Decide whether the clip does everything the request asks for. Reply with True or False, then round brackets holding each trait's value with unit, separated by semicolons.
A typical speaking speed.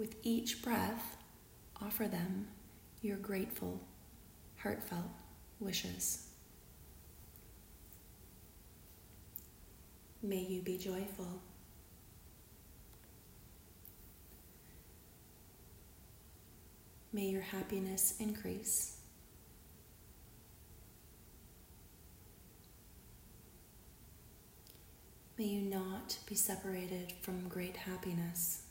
False (50 wpm)